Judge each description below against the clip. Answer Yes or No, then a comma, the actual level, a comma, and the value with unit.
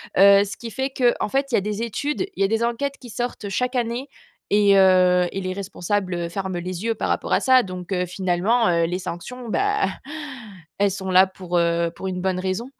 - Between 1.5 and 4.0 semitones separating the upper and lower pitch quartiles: No, average, 4.4 semitones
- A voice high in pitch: Yes, high, 195 Hz